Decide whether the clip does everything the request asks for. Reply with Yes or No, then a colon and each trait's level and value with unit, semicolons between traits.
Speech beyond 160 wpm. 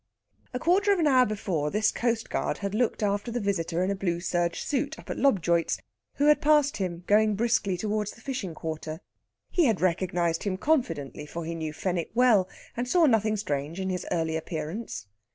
Yes: average, 190 wpm